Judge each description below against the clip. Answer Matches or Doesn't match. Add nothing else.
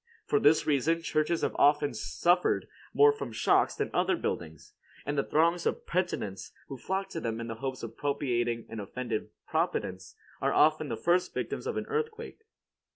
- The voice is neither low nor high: Matches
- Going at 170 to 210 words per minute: Matches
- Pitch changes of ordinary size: Doesn't match